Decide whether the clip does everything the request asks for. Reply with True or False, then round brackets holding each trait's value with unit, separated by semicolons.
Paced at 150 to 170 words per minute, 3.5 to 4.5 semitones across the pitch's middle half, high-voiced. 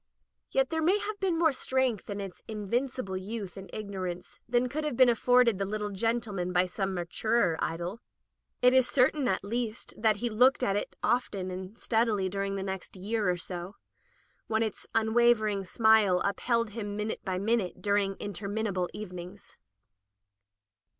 True (165 wpm; 3.8 semitones; 210 Hz)